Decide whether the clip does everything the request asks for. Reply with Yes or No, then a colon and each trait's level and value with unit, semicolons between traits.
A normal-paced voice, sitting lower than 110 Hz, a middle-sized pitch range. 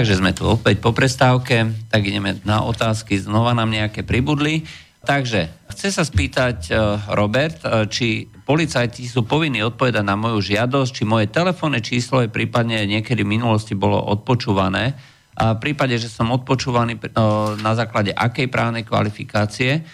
No: average, 150 wpm; low, 115 Hz; average, 3.4 semitones